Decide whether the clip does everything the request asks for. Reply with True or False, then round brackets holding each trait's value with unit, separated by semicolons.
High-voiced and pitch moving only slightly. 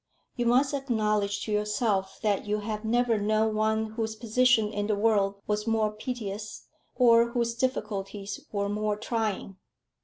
True (215 Hz; 1.9 semitones)